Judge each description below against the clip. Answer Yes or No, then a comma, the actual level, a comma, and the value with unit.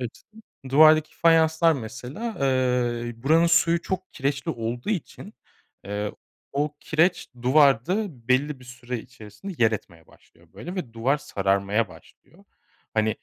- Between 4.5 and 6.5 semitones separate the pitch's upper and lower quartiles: Yes, wide, 5.5 semitones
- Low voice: Yes, low, 130 Hz